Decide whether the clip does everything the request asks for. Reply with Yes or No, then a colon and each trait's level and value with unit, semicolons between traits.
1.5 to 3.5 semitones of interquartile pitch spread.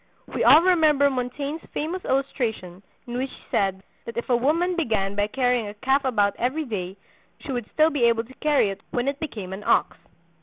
No: wide, 5.6 semitones